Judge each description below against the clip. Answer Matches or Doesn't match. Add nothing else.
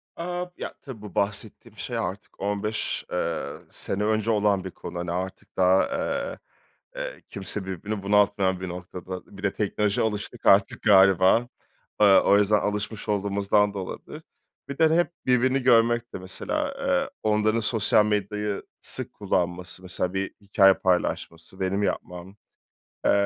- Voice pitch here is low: Matches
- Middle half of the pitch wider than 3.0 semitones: Doesn't match